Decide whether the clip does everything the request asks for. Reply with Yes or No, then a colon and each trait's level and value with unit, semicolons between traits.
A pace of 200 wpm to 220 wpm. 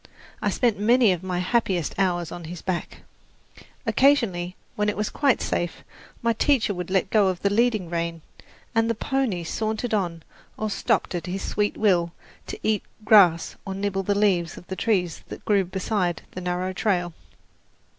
No: average, 170 wpm